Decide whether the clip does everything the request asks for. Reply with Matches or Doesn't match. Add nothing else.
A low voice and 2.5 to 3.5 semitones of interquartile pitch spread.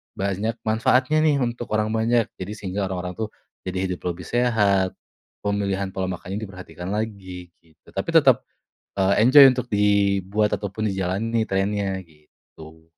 Matches